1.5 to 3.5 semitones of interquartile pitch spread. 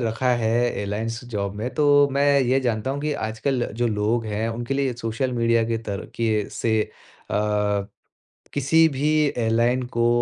Yes: average, 2.8 semitones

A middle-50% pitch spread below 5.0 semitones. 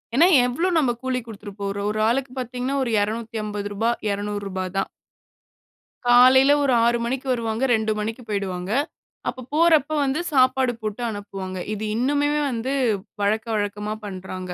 Yes: average, 4.0 semitones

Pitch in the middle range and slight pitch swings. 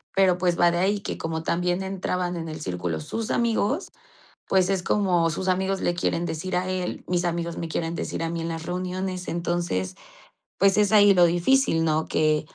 Yes: medium, 175 Hz; narrow, 2.3 semitones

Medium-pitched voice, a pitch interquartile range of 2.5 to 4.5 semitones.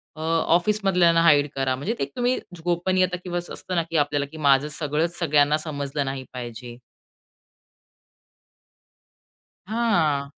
Yes: medium, 160 Hz; average, 3.7 semitones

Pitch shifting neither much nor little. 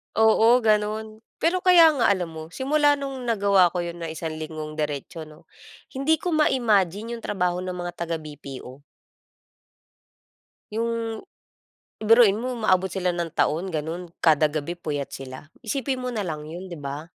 No: wide, 6.3 semitones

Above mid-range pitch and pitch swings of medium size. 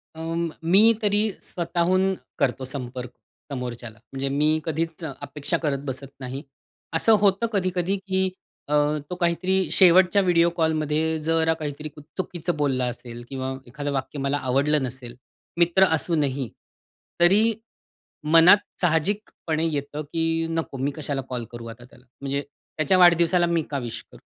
No: medium, 155 Hz; average, 4.3 semitones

